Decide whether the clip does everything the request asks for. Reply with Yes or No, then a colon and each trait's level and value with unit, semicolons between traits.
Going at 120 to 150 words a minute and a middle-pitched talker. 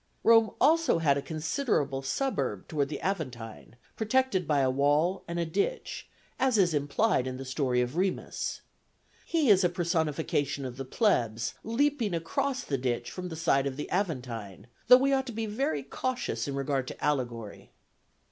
No: average, 170 wpm; medium, 160 Hz